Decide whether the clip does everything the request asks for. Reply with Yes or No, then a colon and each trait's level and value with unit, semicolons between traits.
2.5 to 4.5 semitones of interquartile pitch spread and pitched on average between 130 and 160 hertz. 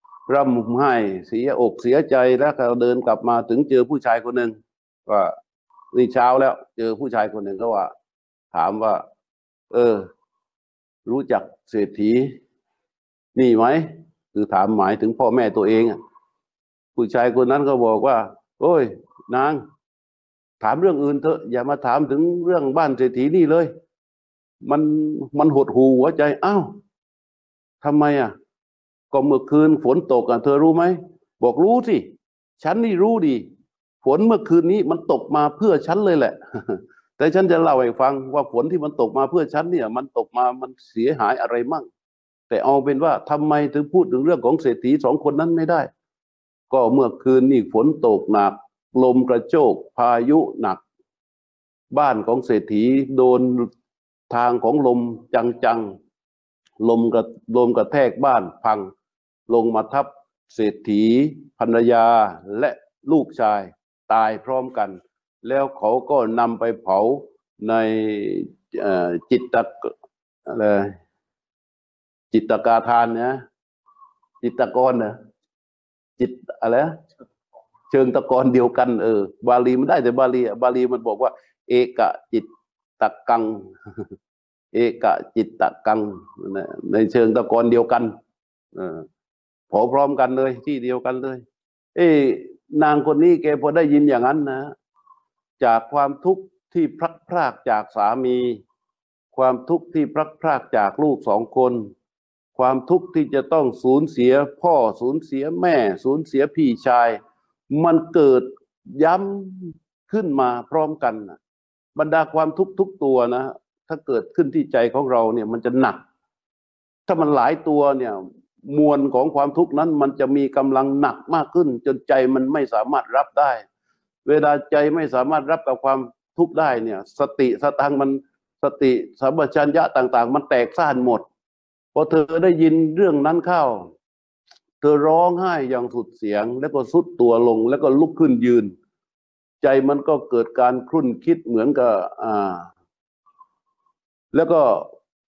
No: average, 5.2 semitones; low, 135 Hz